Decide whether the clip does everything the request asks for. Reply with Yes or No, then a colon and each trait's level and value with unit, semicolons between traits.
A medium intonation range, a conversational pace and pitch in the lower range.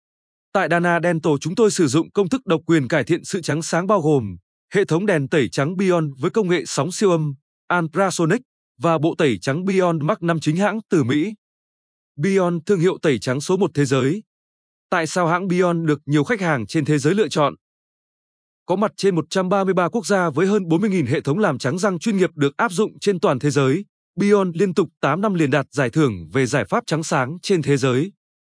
No: average, 4.7 semitones; average, 220 wpm; medium, 170 Hz